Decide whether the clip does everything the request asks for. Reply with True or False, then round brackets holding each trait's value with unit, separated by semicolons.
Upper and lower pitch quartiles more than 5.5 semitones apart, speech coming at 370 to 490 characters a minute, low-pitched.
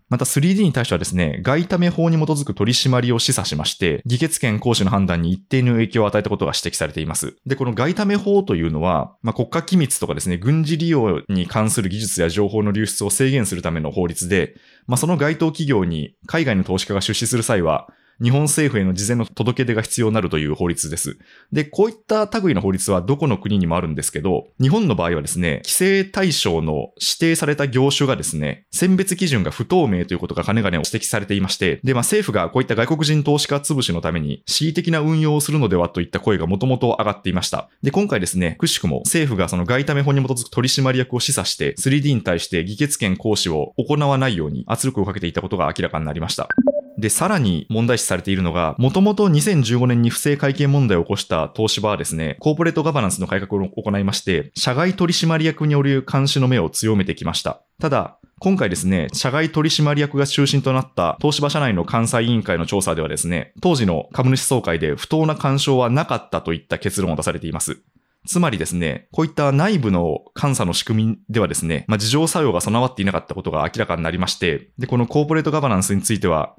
True (7.8 semitones; 440 characters per minute; 120 Hz)